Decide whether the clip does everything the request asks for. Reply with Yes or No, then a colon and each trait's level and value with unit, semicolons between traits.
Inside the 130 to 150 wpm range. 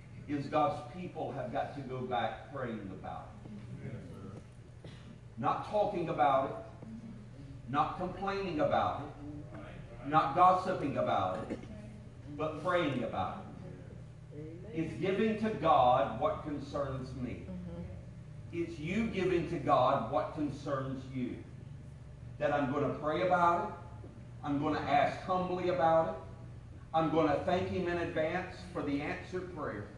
Yes: slow, 135 wpm